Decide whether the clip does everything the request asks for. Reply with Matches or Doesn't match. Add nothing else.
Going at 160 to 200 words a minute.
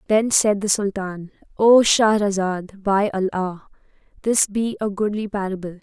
Doesn't match